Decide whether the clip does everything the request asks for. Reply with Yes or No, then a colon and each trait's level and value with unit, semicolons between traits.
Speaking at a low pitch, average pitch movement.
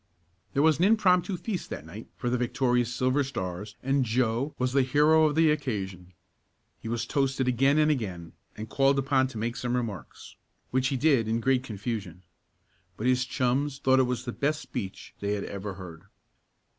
Yes: low, 125 Hz; average, 4.1 semitones